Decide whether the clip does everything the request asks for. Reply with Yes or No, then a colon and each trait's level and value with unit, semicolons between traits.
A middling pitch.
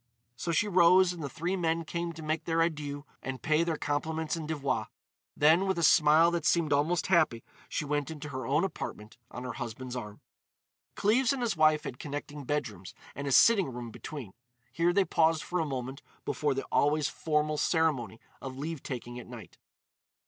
Yes: medium, 155 Hz